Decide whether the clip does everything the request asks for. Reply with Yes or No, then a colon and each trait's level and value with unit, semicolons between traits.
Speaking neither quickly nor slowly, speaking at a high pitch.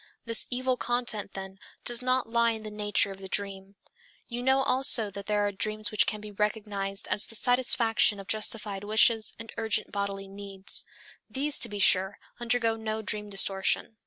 Yes: average, 180 wpm; high, 215 Hz